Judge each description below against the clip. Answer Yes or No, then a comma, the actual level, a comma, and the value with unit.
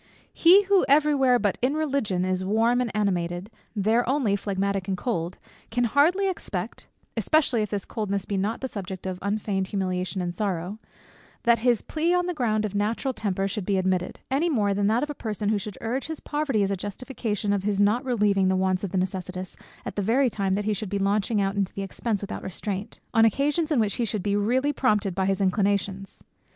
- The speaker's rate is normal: No, fast, 210 wpm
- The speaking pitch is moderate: No, high, 205 Hz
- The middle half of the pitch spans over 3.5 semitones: Yes, average, 4.0 semitones